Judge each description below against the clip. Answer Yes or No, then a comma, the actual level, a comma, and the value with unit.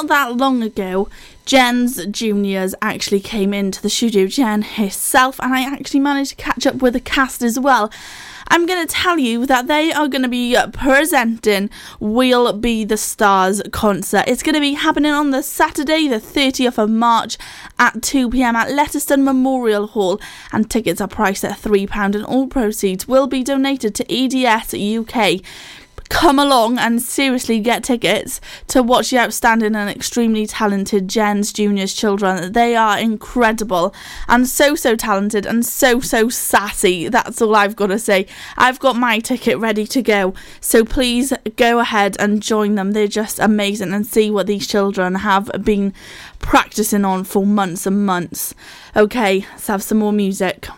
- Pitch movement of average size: Yes, average, 4.2 semitones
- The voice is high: Yes, high, 225 Hz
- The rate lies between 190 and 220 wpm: No, average, 175 wpm